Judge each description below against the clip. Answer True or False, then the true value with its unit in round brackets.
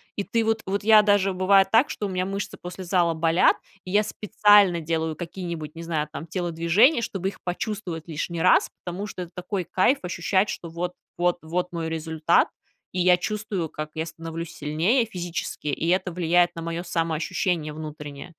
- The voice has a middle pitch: True (175 Hz)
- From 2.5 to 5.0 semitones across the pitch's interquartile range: True (2.9 semitones)